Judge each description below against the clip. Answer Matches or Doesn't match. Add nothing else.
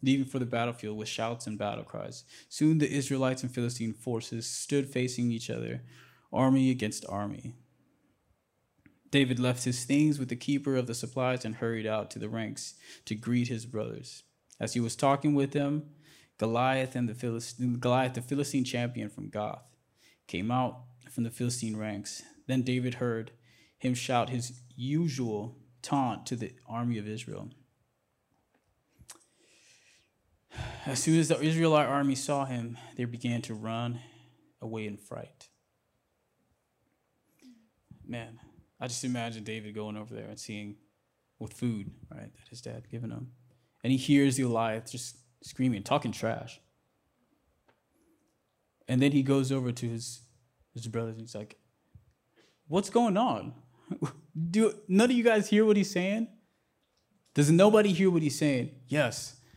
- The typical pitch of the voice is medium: Doesn't match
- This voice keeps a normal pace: Matches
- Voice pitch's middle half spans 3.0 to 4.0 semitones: Matches